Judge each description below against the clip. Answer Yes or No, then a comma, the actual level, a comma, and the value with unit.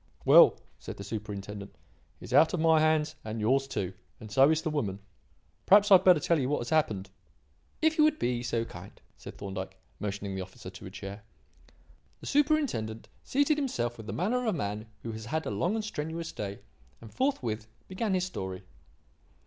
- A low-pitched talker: Yes, low, 130 Hz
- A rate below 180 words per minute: No, average, 195 wpm